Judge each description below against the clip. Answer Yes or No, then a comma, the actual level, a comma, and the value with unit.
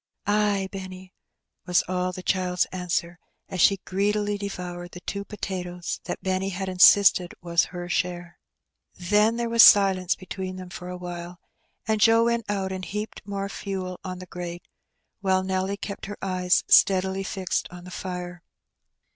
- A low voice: No, medium, 185 Hz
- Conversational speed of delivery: Yes, average, 145 wpm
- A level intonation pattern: Yes, narrow, 1.9 semitones